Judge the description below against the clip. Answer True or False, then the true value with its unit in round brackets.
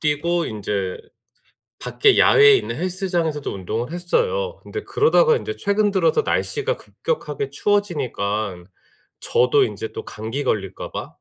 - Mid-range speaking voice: True (170 Hz)